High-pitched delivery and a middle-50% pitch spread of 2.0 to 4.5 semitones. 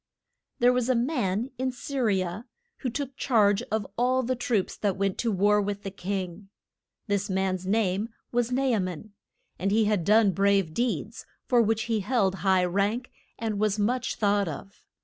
Yes: high, 210 Hz; average, 3.6 semitones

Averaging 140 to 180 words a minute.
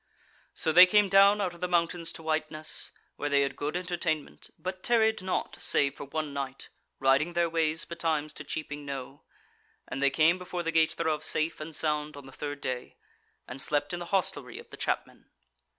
No: average, 195 wpm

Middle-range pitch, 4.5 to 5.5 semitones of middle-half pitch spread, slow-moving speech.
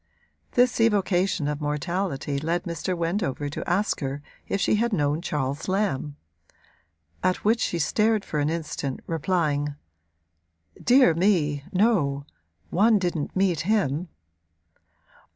Yes: medium, 170 Hz; average, 5.2 semitones; slow, 120 wpm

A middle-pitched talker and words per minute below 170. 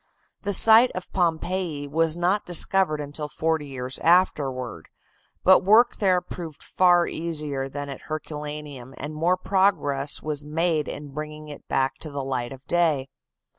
Yes: medium, 155 Hz; average, 150 wpm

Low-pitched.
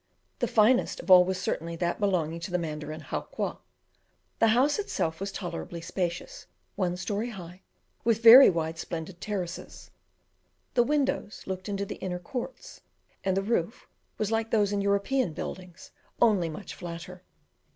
No: high, 190 Hz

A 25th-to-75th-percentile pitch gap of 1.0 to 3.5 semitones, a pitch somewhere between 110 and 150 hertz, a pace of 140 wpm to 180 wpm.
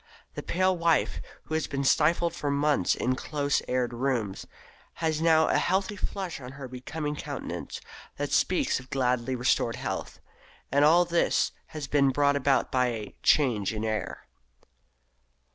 No: average, 4.0 semitones; medium, 140 Hz; average, 155 wpm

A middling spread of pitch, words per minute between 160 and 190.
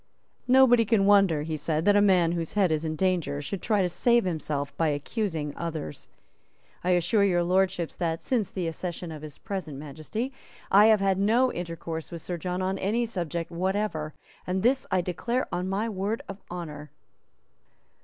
Yes: average, 3.9 semitones; average, 180 wpm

